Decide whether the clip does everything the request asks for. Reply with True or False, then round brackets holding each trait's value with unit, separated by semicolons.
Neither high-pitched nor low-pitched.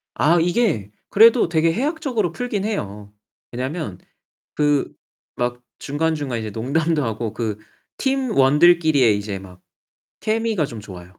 True (150 Hz)